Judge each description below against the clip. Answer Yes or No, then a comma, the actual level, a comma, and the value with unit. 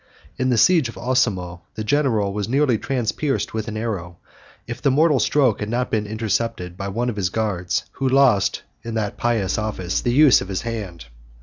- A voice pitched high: No, low, 110 Hz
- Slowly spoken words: No, average, 195 wpm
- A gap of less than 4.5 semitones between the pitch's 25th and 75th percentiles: Yes, average, 4.1 semitones